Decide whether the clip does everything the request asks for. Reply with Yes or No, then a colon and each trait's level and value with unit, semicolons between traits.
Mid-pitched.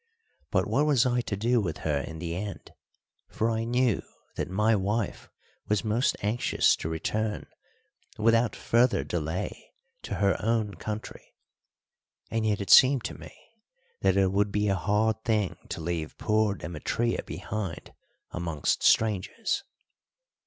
No: low, 105 Hz